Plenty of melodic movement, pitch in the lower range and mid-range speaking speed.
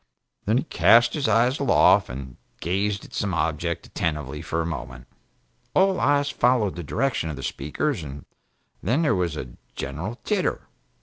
Yes: wide, 8.8 semitones; very low, 95 Hz; average, 165 wpm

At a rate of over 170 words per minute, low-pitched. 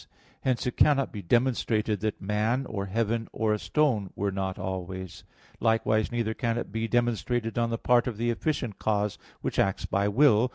Yes: average, 180 wpm; low, 110 Hz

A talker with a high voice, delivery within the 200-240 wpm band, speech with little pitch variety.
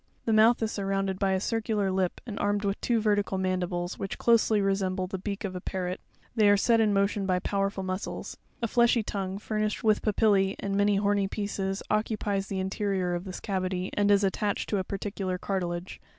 Yes: high, 195 Hz; fast, 205 wpm; narrow, 1.7 semitones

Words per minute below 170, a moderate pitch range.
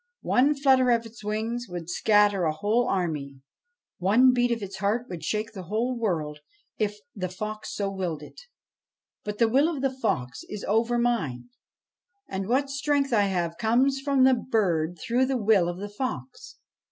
No: average, 175 wpm; average, 5.0 semitones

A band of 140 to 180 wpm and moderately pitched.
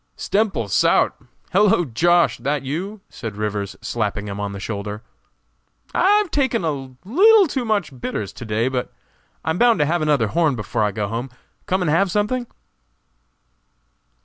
Yes: average, 155 wpm; medium, 150 Hz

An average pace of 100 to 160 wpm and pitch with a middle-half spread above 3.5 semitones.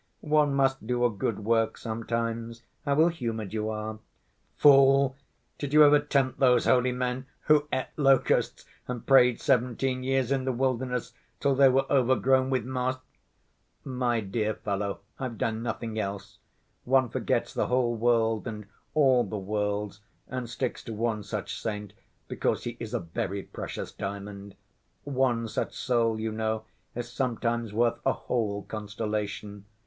No: average, 150 wpm; average, 3.2 semitones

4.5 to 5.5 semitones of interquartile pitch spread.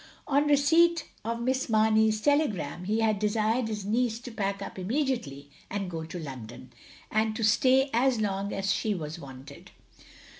Yes: average, 5.1 semitones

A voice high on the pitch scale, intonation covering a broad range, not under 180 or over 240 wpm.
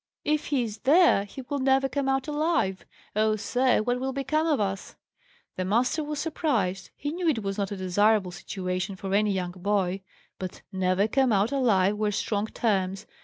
Yes: high, 215 Hz; wide, 5.8 semitones; average, 185 wpm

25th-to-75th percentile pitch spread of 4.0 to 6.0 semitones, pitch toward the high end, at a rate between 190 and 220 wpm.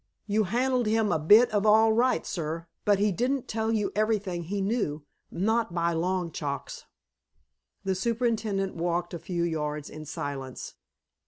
No: average, 4.7 semitones; high, 195 Hz; average, 155 wpm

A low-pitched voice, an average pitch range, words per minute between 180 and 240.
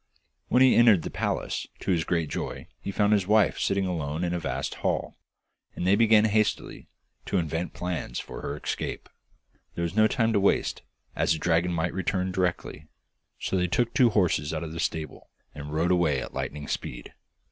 Yes: very low, 90 Hz; average, 4.0 semitones; average, 190 wpm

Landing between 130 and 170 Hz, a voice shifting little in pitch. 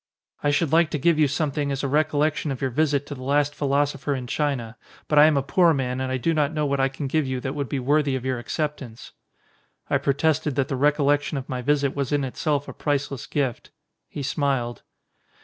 Yes: medium, 140 Hz; narrow, 1.9 semitones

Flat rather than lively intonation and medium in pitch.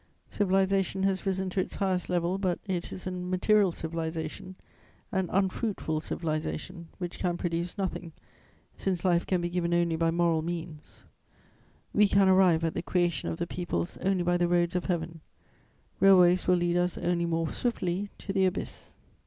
Yes: narrow, 1.9 semitones; medium, 175 Hz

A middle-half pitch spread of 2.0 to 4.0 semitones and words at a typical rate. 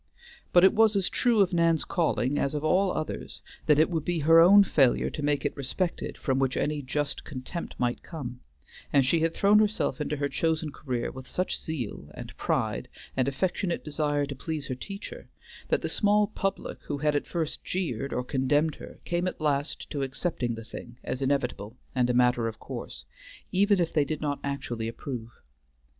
No: average, 4.7 semitones; average, 195 wpm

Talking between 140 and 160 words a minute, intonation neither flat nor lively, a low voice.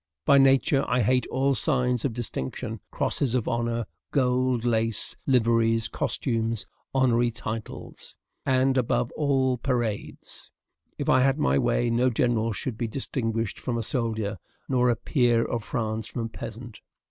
No: average, 150 wpm; narrow, 2.2 semitones; low, 120 Hz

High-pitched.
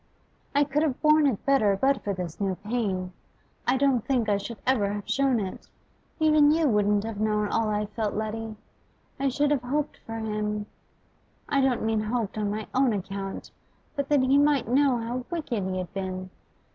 Yes: high, 225 Hz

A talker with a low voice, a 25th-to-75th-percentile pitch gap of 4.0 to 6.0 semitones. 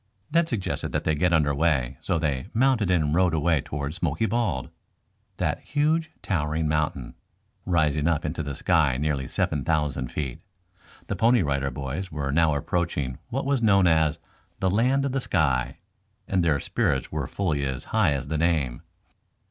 Yes: very low, 80 Hz; average, 4.7 semitones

